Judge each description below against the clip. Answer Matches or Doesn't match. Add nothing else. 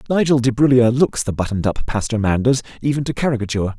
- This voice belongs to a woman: Doesn't match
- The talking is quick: Doesn't match